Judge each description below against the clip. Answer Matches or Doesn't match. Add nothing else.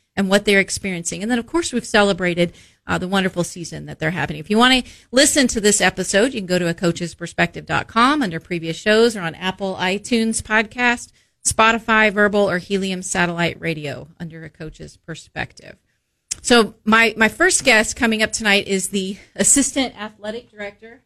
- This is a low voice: Doesn't match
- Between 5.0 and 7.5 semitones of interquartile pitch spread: Doesn't match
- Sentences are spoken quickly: Doesn't match